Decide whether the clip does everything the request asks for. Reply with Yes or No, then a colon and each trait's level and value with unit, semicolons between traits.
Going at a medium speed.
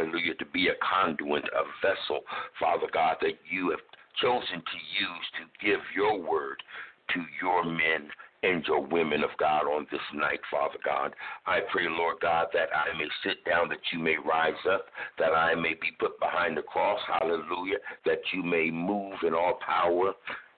Yes: average, 180 wpm